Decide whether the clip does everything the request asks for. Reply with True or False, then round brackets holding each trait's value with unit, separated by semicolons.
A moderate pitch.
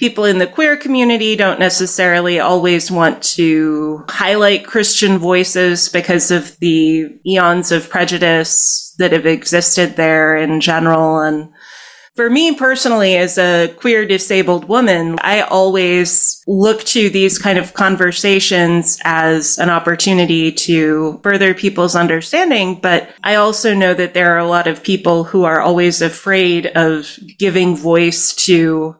True (180 Hz)